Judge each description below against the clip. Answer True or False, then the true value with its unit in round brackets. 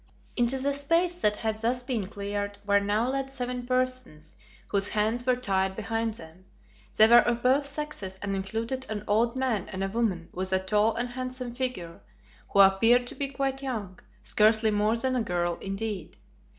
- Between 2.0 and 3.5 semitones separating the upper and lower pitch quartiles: False (4.1 semitones)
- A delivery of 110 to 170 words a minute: False (180 wpm)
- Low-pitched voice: False (225 Hz)